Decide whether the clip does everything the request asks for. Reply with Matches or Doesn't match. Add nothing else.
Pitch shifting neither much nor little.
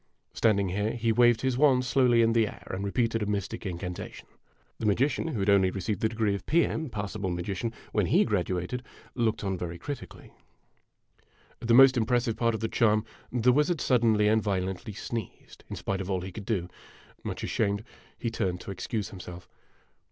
Matches